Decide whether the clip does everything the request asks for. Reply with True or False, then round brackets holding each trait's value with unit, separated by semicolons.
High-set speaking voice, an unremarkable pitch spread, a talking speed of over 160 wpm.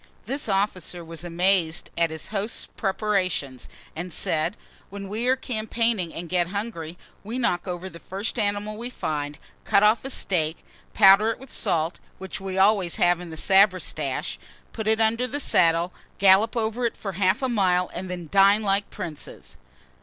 True (195 Hz; 3.7 semitones; 170 wpm)